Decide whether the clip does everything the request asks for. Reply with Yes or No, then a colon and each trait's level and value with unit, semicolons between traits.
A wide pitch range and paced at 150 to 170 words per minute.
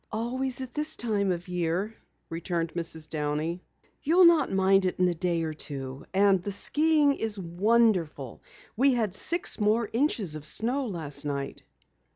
Yes: wide, 6.2 semitones; average, 160 wpm